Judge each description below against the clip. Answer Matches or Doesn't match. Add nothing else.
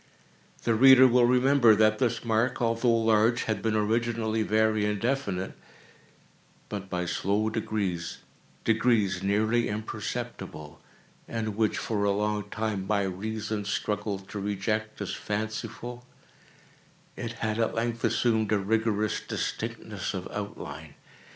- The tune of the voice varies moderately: Doesn't match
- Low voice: Matches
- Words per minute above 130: Doesn't match